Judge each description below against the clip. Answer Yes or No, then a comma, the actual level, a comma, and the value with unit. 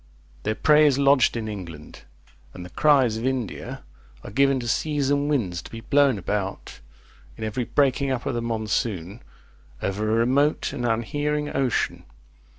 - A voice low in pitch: Yes, low, 120 Hz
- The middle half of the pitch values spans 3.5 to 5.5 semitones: Yes, average, 4.6 semitones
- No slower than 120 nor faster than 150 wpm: No, average, 160 wpm